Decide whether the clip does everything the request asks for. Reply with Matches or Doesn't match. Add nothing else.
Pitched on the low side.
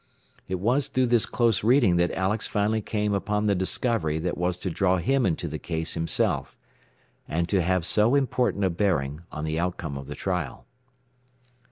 Matches